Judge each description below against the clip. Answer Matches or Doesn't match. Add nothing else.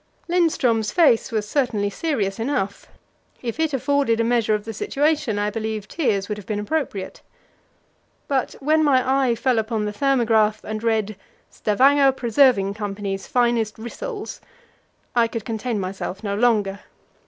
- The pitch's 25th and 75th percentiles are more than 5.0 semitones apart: Doesn't match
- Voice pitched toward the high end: Matches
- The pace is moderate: Matches